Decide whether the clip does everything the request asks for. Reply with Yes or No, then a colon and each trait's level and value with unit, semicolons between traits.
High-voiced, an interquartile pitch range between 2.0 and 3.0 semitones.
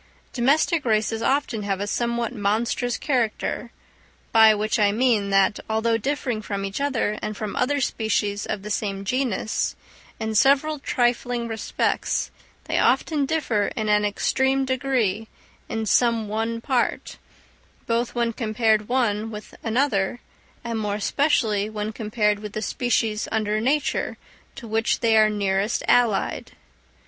Yes: high, 225 Hz; average, 2.7 semitones